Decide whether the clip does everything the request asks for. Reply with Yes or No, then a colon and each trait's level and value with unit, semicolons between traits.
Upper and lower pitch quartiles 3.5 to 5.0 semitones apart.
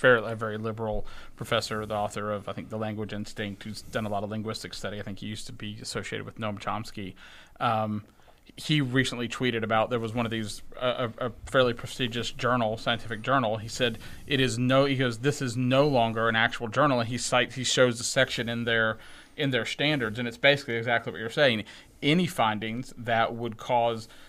No: average, 2.7 semitones